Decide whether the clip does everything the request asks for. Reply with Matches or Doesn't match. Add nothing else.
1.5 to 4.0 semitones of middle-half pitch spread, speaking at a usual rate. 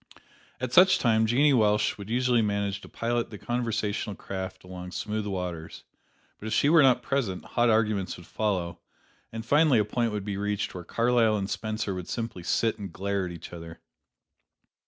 Matches